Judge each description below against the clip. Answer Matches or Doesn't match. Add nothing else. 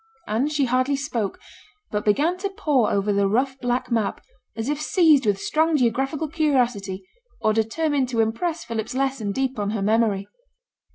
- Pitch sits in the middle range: Doesn't match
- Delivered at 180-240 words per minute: Doesn't match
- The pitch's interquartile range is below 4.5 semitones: Doesn't match